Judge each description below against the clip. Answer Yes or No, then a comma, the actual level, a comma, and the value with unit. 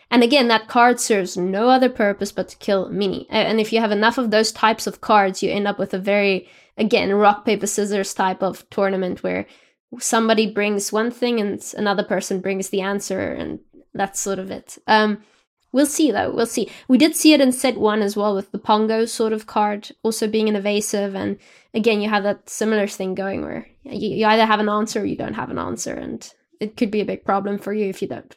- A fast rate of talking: Yes, fast, 230 wpm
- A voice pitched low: No, high, 210 Hz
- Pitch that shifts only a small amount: Yes, narrow, 2.1 semitones